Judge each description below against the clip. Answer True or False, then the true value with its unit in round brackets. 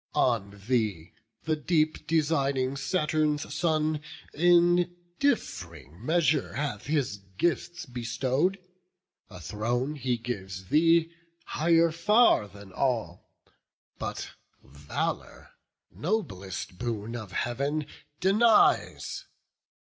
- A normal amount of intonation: False (7.4 semitones)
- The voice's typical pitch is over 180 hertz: False (140 Hz)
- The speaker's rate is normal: False (90 wpm)